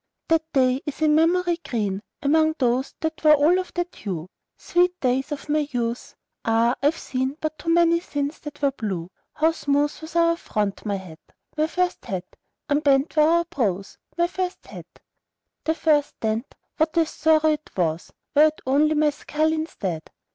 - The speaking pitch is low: No, very high, 300 Hz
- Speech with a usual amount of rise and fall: Yes, average, 4.5 semitones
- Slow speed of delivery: No, average, 175 wpm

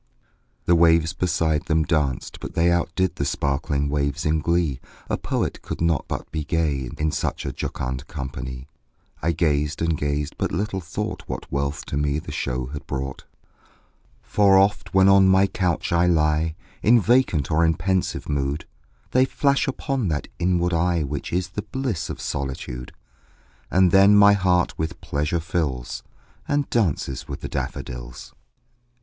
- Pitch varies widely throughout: No, average, 4.2 semitones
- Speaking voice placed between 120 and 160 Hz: No, very low, 80 Hz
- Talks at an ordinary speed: Yes, average, 160 wpm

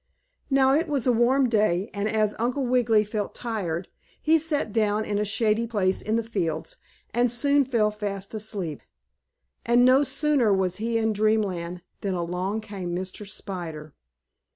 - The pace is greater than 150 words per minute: Yes, average, 160 wpm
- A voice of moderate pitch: No, high, 215 Hz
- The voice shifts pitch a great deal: No, average, 3.9 semitones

